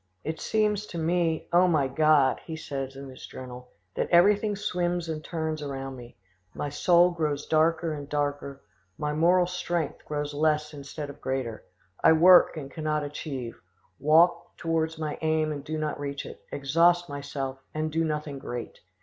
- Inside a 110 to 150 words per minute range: No, average, 165 wpm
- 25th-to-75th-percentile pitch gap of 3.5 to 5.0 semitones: No, average, 2.9 semitones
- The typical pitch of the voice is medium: Yes, medium, 155 Hz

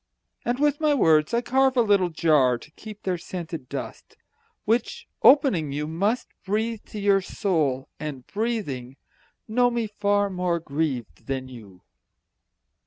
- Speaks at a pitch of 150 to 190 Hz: Yes, medium, 185 Hz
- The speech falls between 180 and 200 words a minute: No, average, 145 wpm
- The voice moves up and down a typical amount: No, wide, 7.0 semitones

